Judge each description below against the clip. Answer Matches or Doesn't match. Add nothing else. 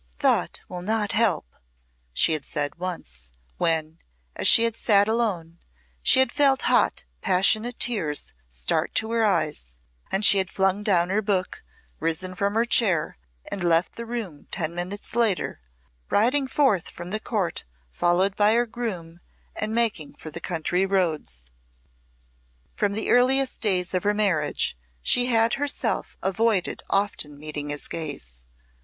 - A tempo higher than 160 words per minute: Doesn't match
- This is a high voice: Matches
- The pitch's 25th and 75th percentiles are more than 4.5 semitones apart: Matches